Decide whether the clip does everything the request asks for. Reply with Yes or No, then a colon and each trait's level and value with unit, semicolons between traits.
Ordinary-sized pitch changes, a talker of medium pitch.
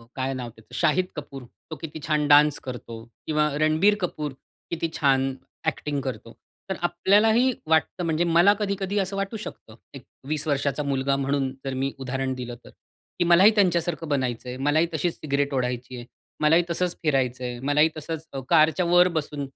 Yes: average, 4.2 semitones; medium, 150 Hz